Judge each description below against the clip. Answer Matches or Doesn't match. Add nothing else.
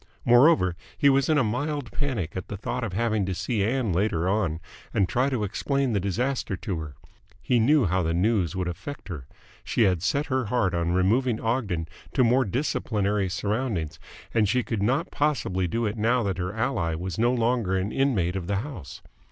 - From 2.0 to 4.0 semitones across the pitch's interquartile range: Doesn't match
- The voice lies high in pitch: Doesn't match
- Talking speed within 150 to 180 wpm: Doesn't match